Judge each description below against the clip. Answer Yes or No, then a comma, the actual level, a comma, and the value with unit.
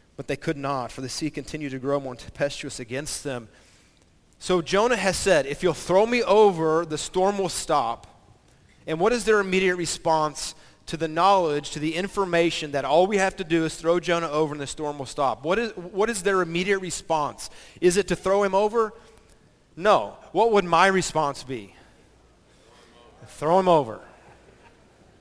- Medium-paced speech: Yes, average, 180 wpm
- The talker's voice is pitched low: No, medium, 165 Hz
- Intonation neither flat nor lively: Yes, average, 4.9 semitones